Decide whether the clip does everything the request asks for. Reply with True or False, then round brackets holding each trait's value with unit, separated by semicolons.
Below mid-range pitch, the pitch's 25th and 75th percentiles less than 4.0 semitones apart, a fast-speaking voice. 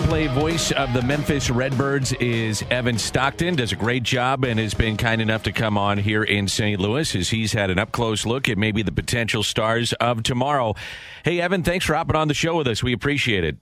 False (120 Hz; 4.3 semitones; 230 wpm)